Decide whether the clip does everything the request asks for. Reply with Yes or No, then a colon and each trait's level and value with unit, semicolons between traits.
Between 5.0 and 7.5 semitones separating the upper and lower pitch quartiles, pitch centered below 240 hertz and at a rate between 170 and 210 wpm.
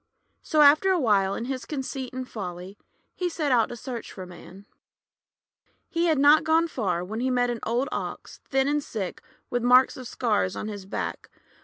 No: wide, 5.4 semitones; very high, 250 Hz; average, 190 wpm